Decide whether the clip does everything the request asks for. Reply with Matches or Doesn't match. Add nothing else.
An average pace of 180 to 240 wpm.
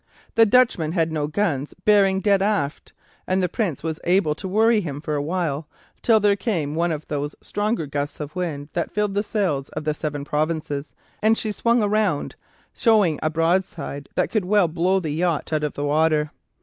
Matches